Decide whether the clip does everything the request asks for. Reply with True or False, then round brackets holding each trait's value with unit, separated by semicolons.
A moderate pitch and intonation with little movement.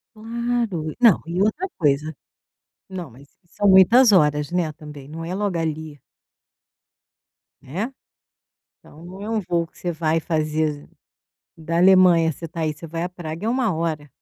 False (165 Hz; 3.5 semitones)